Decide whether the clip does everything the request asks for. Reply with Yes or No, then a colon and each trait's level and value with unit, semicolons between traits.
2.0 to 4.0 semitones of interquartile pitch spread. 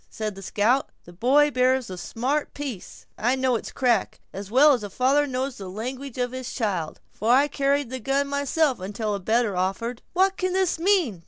No: average, 4.8 semitones